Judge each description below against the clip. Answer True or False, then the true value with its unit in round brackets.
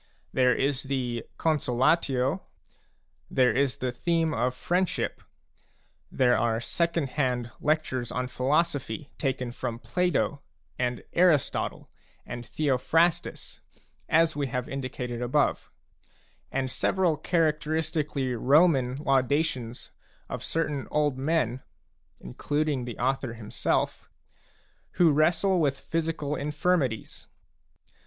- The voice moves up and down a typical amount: True (3.9 semitones)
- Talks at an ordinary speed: False (105 wpm)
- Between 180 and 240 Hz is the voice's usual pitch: False (135 Hz)